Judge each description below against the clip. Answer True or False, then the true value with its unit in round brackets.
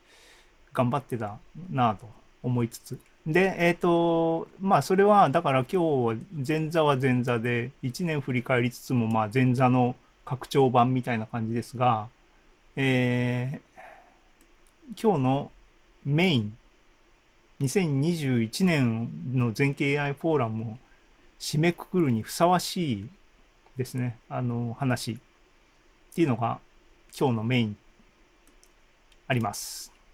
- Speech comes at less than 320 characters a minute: True (215 characters per minute)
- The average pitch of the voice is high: False (130 Hz)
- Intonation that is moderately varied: True (4.7 semitones)